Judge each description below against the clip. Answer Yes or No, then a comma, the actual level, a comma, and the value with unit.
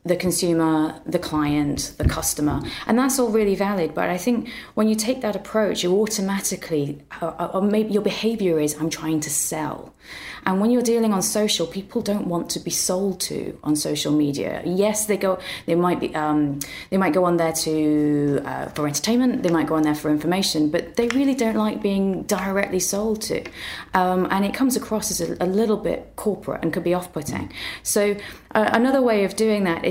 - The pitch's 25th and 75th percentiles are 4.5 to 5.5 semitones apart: Yes, average, 4.8 semitones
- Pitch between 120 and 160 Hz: No, medium, 185 Hz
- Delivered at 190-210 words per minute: Yes, fast, 205 wpm